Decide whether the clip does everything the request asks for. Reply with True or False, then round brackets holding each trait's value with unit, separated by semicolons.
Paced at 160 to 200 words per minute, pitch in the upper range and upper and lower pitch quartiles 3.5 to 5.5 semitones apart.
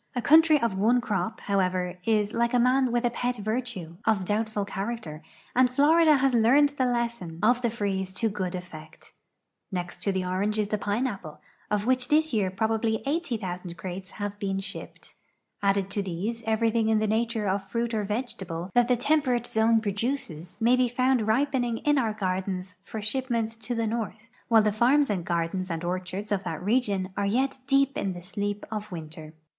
True (185 wpm; 215 Hz; 4.2 semitones)